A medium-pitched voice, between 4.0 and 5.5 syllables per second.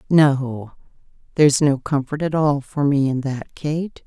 Yes: medium, 145 Hz; 4.1 syllables/s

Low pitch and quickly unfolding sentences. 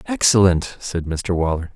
No: very low, 95 Hz; slow, 135 wpm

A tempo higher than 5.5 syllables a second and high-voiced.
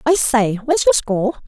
Yes: 6.1 syllables/s; high, 240 Hz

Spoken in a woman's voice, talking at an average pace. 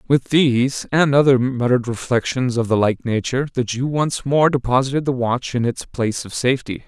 No: male; average, 190 wpm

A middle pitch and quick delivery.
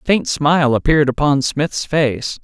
No: medium, 145 Hz; average, 175 wpm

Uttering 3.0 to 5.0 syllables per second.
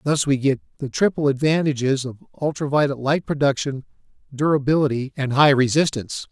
No: 5.6 syllables/s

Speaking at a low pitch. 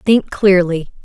No: medium, 185 Hz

